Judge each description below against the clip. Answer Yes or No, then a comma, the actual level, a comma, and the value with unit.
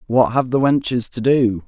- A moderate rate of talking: No, fast, 215 wpm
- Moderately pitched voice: No, low, 120 Hz